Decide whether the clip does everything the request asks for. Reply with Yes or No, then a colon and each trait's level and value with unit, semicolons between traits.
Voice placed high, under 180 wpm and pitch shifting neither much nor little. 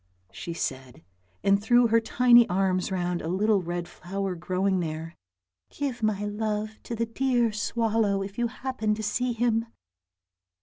Yes: high, 210 Hz; average, 160 wpm; average, 4.0 semitones